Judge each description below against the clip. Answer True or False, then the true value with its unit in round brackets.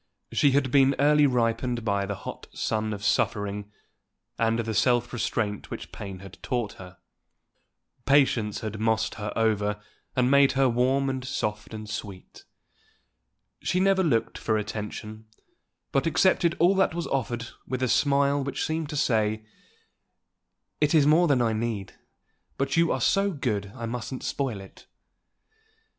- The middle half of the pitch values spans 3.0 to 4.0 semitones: False (4.5 semitones)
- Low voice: True (120 Hz)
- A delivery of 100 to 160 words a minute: True (150 wpm)